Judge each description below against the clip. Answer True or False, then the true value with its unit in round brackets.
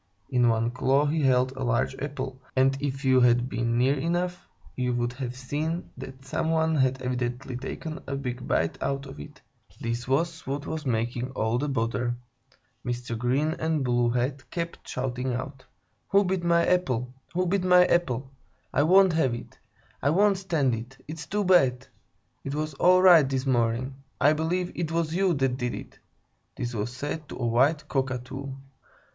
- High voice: False (135 Hz)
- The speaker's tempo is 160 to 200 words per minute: True (180 wpm)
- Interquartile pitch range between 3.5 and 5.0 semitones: True (4.3 semitones)